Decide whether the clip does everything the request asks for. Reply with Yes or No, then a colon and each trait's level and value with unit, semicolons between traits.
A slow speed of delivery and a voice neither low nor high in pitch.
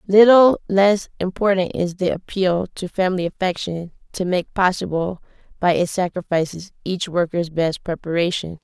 Yes: slow, 130 wpm; medium, 180 Hz